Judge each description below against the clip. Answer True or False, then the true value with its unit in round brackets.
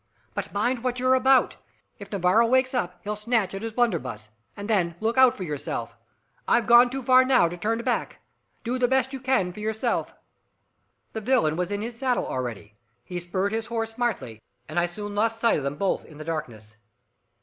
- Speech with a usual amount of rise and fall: False (5.7 semitones)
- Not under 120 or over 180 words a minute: False (200 wpm)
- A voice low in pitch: False (220 Hz)